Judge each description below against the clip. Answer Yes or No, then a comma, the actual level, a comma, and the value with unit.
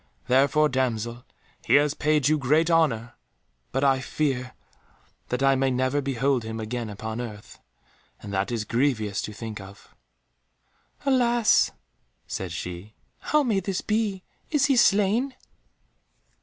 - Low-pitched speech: Yes, low, 130 Hz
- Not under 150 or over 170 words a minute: No, slow, 135 wpm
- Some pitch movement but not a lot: No, wide, 6.4 semitones